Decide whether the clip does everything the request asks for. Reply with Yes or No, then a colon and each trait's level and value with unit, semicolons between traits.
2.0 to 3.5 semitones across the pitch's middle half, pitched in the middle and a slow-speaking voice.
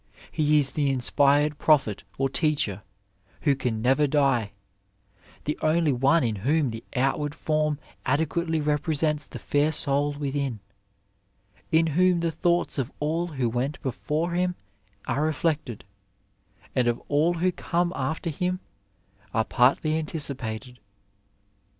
Yes: average, 3.1 semitones; medium, 145 Hz; slow, 130 wpm